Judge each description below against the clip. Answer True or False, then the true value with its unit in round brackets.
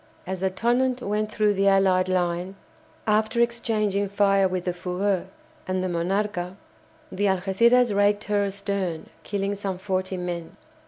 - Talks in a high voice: True (195 Hz)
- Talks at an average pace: True (145 wpm)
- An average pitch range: False (2.0 semitones)